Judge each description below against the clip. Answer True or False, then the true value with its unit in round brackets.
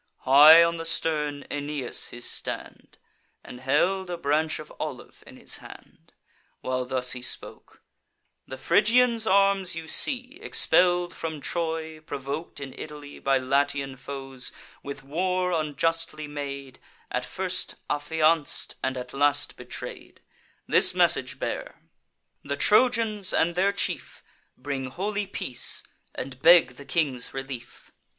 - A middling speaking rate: False (130 wpm)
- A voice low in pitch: False (150 Hz)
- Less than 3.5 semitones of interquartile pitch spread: False (4.5 semitones)